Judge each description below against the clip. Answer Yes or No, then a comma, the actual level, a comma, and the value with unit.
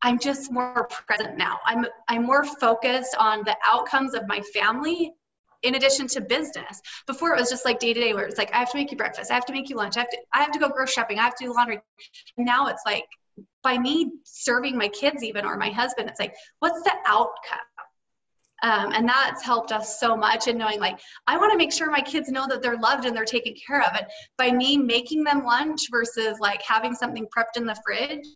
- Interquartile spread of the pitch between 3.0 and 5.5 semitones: Yes, average, 3.5 semitones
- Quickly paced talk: Yes, fast, 235 wpm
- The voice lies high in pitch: Yes, high, 245 Hz